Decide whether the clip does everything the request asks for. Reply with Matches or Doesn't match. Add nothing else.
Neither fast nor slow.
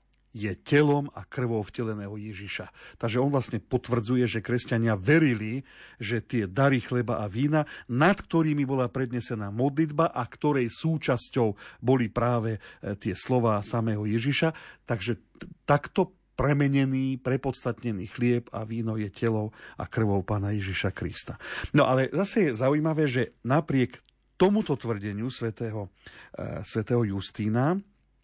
Matches